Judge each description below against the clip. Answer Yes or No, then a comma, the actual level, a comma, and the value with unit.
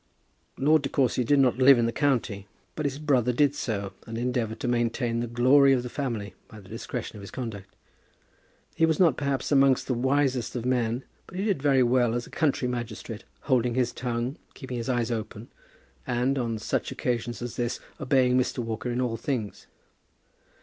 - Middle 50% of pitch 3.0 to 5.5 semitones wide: No, narrow, 2.5 semitones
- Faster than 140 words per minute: Yes, average, 190 wpm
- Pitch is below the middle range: Yes, low, 125 Hz